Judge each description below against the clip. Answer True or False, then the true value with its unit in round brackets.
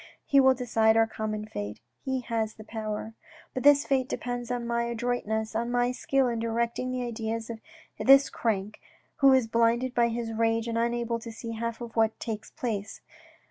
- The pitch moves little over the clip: True (1.6 semitones)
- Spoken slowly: False (185 wpm)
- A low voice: False (230 Hz)